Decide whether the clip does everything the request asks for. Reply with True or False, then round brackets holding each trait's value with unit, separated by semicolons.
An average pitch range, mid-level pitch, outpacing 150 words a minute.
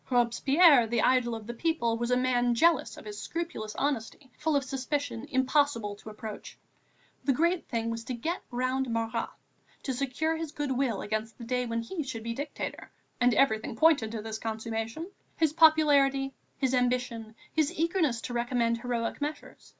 False (4.0 semitones; 250 Hz; 175 wpm)